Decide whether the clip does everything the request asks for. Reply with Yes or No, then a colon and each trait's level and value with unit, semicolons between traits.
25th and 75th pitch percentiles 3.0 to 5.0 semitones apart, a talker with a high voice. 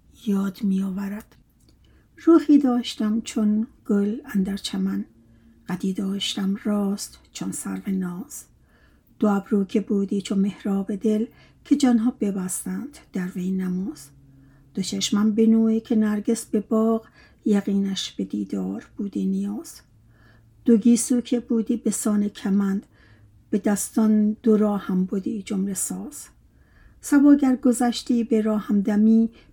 No: narrow, 2.6 semitones; high, 210 Hz